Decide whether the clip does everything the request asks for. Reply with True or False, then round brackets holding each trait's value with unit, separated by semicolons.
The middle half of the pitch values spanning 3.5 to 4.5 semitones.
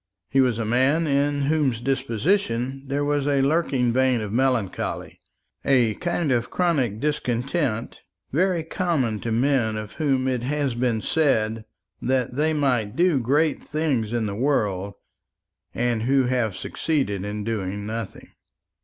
True (4.2 semitones)